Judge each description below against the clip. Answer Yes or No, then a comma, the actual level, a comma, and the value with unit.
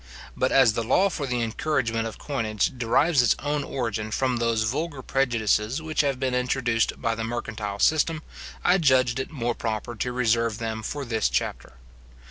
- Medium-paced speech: Yes, average, 170 wpm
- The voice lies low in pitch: Yes, low, 120 Hz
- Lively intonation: No, average, 3.2 semitones